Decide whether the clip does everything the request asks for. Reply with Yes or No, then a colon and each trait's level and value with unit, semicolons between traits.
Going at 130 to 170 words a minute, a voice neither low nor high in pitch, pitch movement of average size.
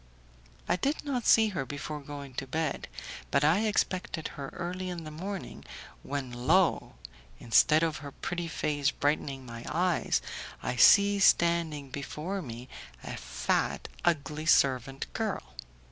Yes: average, 140 wpm; medium, 155 Hz; average, 4.5 semitones